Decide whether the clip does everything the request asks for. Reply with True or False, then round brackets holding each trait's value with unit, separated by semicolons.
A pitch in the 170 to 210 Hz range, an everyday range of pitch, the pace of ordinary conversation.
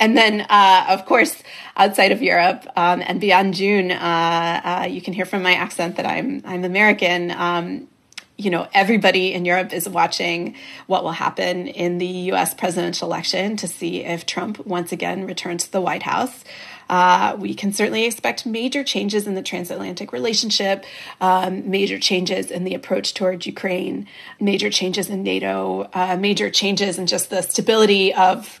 False (185 Hz; 2.2 semitones; 170 wpm)